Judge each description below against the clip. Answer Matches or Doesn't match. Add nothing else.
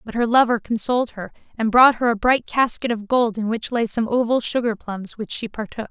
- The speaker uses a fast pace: Matches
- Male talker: Doesn't match